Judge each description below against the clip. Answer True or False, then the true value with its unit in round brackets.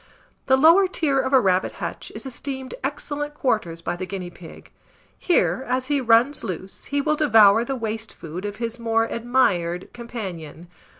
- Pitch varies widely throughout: True (6.1 semitones)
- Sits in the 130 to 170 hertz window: False (235 Hz)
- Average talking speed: True (170 wpm)